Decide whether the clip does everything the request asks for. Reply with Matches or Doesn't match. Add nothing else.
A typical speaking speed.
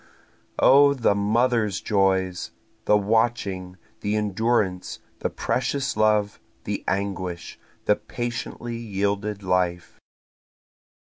Doesn't match